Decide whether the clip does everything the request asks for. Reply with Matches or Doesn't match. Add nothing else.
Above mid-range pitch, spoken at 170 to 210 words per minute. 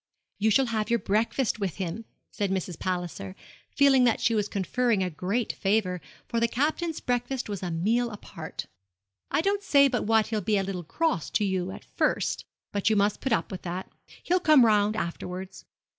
Matches